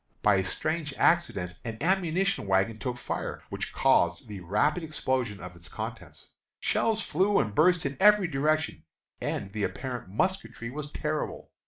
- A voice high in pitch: No, low, 135 Hz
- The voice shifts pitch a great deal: Yes, wide, 8.6 semitones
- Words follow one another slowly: No, average, 155 wpm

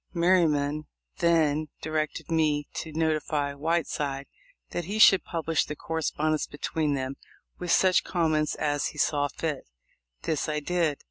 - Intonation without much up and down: Yes, narrow, 2.1 semitones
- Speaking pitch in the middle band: Yes, medium, 155 Hz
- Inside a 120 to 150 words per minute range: Yes, slow, 135 wpm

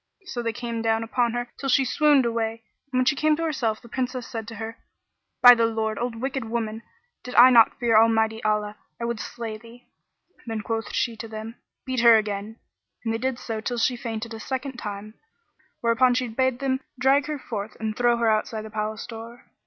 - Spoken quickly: Yes, fast, 215 wpm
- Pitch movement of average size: No, narrow, 2.1 semitones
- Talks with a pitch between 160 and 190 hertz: No, high, 230 Hz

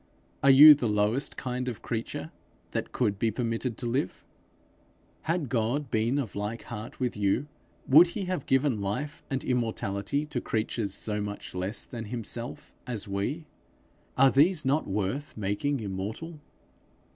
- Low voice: Yes, low, 120 Hz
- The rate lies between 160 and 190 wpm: No, average, 150 wpm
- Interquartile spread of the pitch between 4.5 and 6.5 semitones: Yes, average, 5.1 semitones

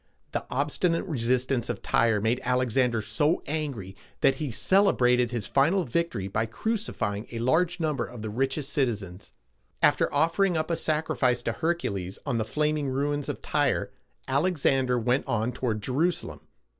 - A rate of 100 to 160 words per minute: Yes, average, 155 wpm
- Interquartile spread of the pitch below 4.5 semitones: No, average, 5.0 semitones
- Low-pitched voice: Yes, low, 130 Hz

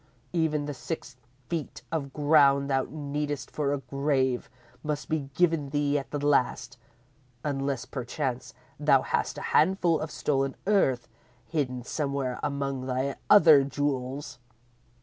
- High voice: No, medium, 140 Hz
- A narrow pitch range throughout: Yes, narrow, 2.0 semitones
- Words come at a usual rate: No, slow, 130 wpm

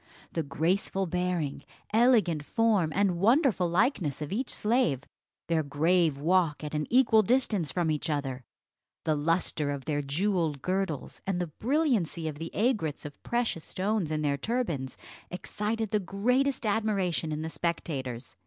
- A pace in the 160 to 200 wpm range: No, average, 150 wpm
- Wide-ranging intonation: Yes, wide, 6.0 semitones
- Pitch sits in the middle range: Yes, medium, 175 Hz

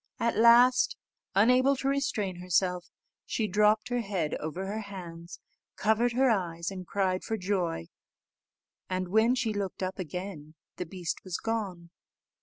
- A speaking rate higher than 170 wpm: No, average, 145 wpm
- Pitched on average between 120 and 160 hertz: No, high, 195 Hz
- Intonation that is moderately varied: Yes, average, 3.9 semitones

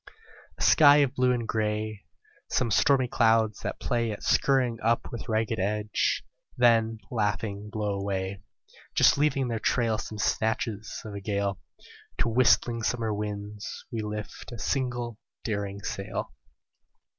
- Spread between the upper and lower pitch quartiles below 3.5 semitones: Yes, narrow, 2.5 semitones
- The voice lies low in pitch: Yes, low, 110 Hz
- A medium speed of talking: Yes, average, 145 wpm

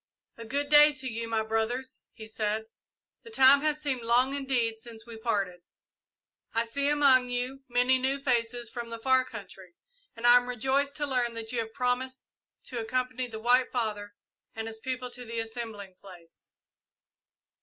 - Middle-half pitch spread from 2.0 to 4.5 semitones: Yes, narrow, 2.6 semitones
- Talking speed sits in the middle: Yes, average, 175 wpm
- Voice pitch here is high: Yes, high, 245 Hz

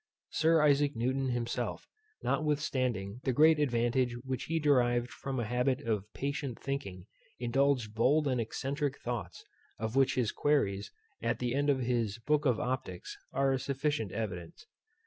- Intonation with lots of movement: No, average, 3.3 semitones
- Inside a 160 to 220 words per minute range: No, average, 150 wpm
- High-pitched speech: No, low, 130 Hz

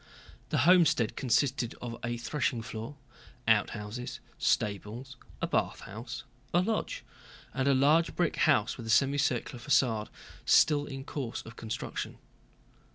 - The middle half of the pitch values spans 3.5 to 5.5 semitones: Yes, average, 4.0 semitones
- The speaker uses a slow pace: Yes, slow, 120 wpm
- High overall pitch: No, low, 125 Hz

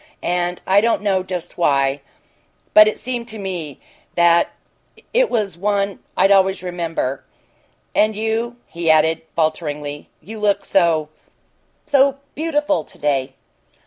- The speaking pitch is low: No, medium, 185 Hz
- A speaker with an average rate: No, slow, 130 wpm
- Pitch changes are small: No, average, 5.0 semitones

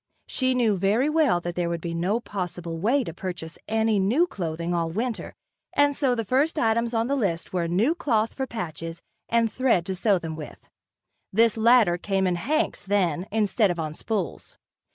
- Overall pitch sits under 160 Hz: No, high, 205 Hz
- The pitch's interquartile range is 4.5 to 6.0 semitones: Yes, average, 5.3 semitones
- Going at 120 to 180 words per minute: No, average, 190 wpm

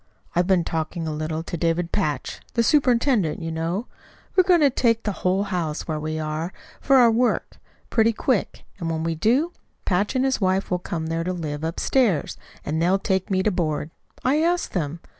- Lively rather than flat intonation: Yes, wide, 6.1 semitones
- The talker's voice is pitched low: No, medium, 180 Hz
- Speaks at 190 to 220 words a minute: Yes, average, 195 wpm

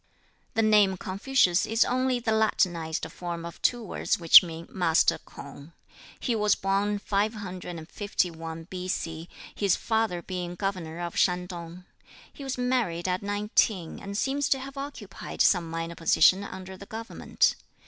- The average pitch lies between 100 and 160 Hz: No, high, 190 Hz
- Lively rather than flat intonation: No, average, 4.2 semitones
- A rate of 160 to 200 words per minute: No, average, 140 wpm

